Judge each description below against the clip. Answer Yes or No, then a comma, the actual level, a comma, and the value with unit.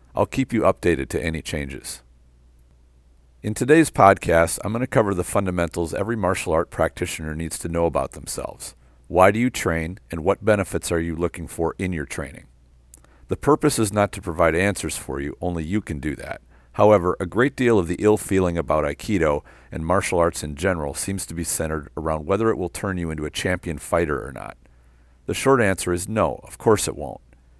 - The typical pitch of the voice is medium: No, very low, 85 Hz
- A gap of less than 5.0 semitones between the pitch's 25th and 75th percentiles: No, average, 5.3 semitones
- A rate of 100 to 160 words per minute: No, average, 200 wpm